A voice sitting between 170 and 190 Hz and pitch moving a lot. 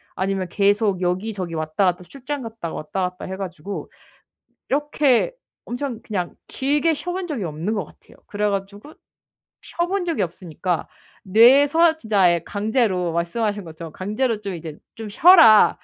No: high, 205 Hz; wide, 6.5 semitones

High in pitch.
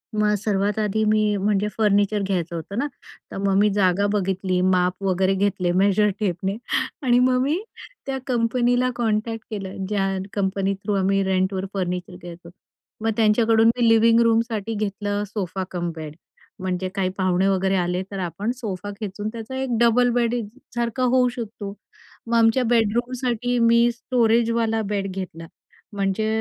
Yes: high, 205 Hz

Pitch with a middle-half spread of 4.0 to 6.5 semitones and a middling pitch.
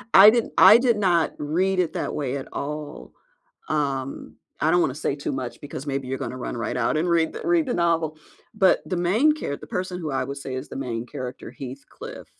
Yes: average, 5.3 semitones; medium, 150 Hz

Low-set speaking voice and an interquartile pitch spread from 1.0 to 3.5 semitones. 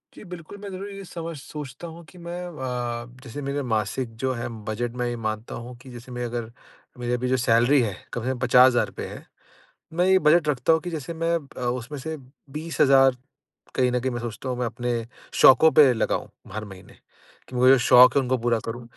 No: low, 125 Hz; average, 4.1 semitones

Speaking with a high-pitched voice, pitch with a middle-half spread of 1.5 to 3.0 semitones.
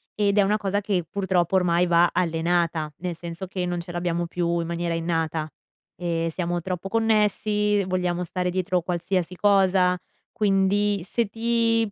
No: medium, 180 Hz; average, 2.7 semitones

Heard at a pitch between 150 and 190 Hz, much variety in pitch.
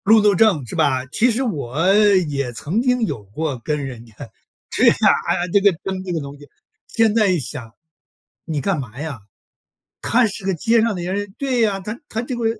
Yes: medium, 185 Hz; wide, 7.3 semitones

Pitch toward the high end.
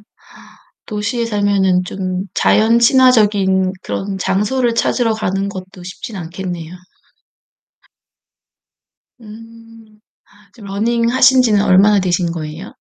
Yes: high, 205 Hz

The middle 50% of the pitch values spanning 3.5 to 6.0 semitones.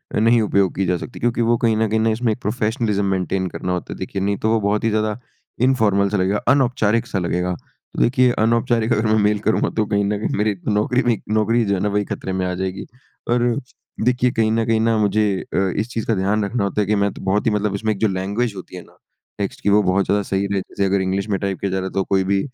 No: narrow, 2.5 semitones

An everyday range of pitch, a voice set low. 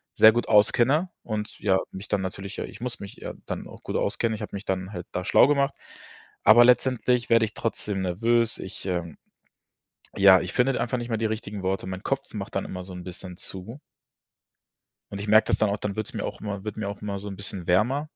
Yes: average, 3.6 semitones; low, 105 Hz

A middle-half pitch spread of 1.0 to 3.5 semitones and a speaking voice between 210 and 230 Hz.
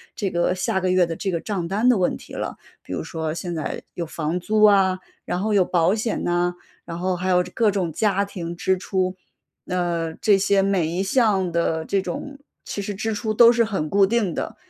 No: average, 2.8 semitones; medium, 185 Hz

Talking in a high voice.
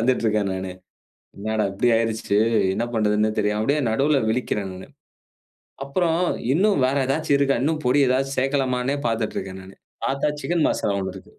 No: low, 125 Hz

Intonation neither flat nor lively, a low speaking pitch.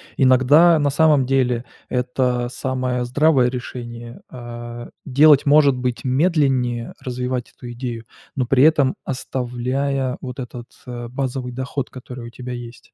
No: narrow, 1.8 semitones; low, 125 Hz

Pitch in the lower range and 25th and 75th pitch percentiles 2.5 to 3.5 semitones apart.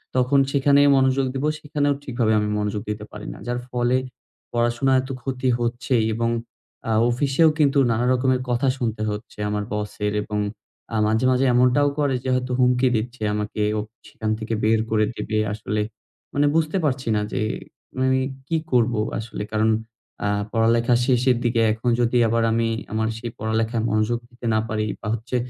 Yes: low, 120 Hz; average, 2.9 semitones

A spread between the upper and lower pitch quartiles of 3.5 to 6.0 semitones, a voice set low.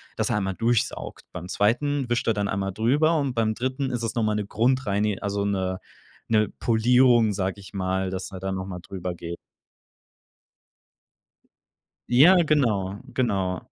Yes: average, 4.2 semitones; low, 105 Hz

